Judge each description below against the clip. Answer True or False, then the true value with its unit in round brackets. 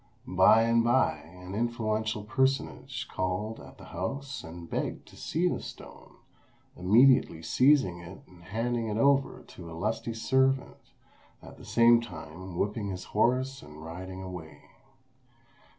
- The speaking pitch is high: False (110 Hz)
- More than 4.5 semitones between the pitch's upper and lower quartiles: True (5.2 semitones)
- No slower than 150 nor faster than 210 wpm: False (140 wpm)